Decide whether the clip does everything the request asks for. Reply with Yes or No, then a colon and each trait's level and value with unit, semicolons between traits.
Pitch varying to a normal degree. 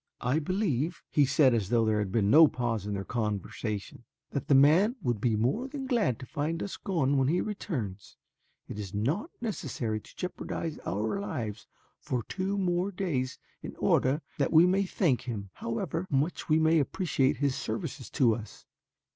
No: wide, 7.5 semitones